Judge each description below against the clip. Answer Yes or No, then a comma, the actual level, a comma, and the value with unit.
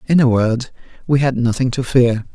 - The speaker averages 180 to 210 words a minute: Yes, fast, 205 wpm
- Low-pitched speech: Yes, low, 125 Hz